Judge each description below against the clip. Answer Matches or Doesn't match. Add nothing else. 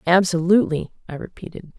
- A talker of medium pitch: Matches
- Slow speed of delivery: Matches